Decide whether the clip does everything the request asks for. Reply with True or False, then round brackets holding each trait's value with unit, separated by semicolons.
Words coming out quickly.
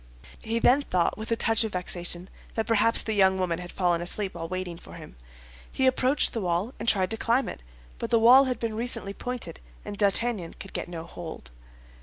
True (210 wpm)